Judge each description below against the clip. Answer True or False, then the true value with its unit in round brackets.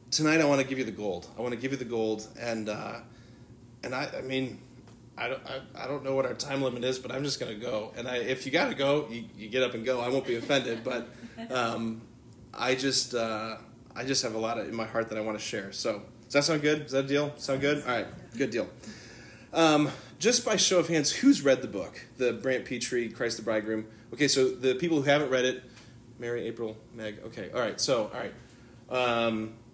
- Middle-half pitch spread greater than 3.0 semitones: False (2.7 semitones)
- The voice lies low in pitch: True (125 Hz)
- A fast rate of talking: True (250 wpm)